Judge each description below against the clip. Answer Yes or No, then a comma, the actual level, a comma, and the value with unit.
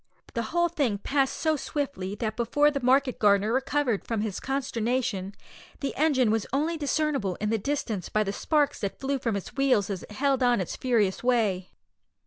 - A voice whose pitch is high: Yes, high, 245 Hz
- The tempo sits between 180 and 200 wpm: Yes, average, 190 wpm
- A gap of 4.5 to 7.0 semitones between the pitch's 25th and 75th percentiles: Yes, average, 5.0 semitones